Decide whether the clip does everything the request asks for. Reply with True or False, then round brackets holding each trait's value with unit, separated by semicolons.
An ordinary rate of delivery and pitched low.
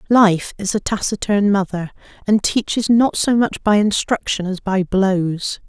False (160 wpm; 200 Hz)